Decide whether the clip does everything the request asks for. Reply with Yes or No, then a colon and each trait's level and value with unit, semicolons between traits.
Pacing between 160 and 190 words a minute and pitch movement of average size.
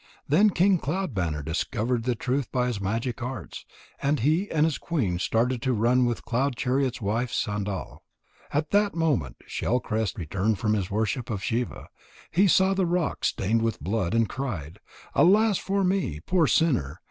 No: average, 170 wpm; wide, 7.2 semitones